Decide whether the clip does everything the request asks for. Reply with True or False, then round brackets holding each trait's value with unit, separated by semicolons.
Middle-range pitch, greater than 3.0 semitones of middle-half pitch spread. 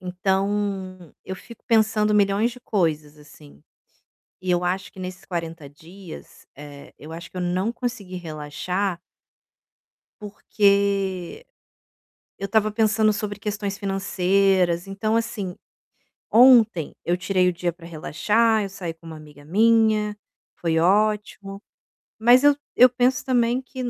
False (195 Hz; 3.5 semitones)